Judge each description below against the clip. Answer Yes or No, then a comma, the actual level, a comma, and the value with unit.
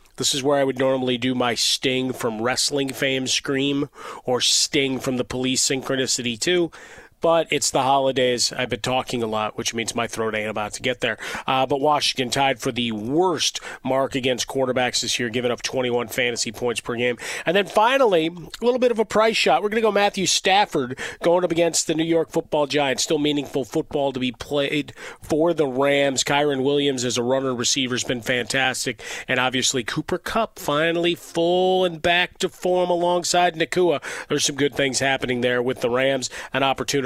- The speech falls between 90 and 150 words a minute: No, average, 200 wpm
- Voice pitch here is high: No, low, 135 Hz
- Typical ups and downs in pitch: Yes, average, 4.2 semitones